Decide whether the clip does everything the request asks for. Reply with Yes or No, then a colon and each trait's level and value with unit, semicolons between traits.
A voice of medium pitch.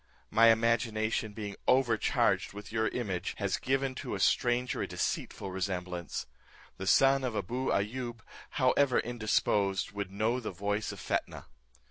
No: low, 110 Hz